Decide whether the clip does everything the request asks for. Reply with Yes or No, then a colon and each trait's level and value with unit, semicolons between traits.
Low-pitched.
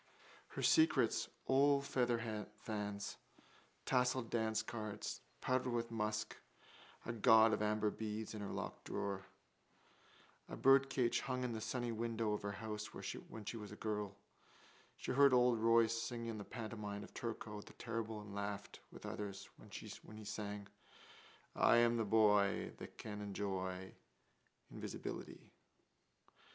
Yes: low, 110 Hz